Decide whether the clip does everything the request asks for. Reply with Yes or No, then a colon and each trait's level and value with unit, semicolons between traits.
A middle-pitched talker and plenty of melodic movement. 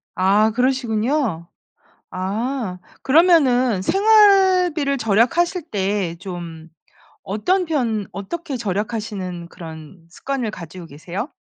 No: high, 220 Hz; wide, 7.1 semitones